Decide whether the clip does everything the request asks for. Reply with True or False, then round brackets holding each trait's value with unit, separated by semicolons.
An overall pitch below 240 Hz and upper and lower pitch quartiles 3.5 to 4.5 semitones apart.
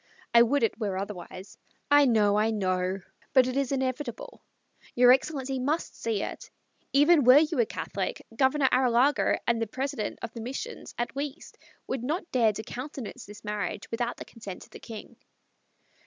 False (245 Hz; 4.2 semitones)